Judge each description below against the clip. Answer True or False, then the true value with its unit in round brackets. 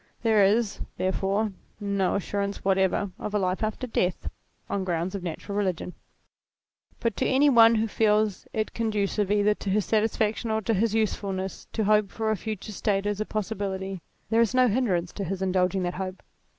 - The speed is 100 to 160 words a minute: False (180 wpm)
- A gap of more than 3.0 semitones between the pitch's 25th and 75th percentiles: False (2.4 semitones)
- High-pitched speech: True (205 Hz)